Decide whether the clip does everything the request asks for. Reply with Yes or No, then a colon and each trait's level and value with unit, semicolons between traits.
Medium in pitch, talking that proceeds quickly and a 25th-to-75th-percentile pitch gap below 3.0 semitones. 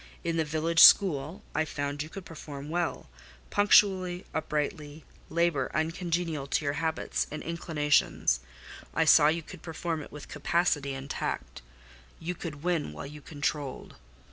No: medium, 155 Hz; average, 145 wpm; narrow, 2.5 semitones